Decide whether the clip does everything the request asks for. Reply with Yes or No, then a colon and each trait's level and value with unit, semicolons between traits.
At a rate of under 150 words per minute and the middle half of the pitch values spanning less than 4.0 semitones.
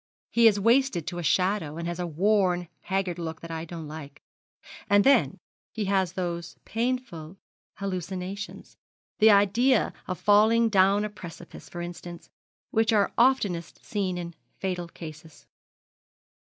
Yes: average, 140 wpm; average, 3.5 semitones